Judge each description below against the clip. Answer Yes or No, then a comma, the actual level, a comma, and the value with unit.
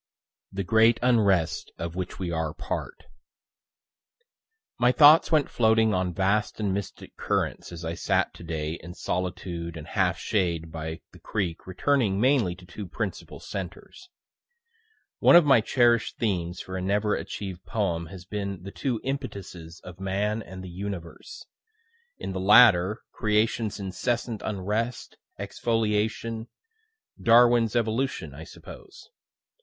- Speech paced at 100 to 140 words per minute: Yes, slow, 135 wpm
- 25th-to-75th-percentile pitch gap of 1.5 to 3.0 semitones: No, average, 4.3 semitones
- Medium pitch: No, low, 100 Hz